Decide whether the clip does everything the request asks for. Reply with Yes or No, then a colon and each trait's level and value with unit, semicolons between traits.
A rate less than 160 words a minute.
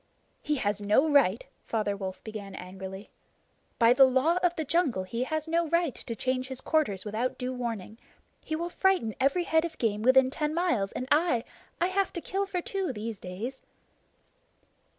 No: average, 180 wpm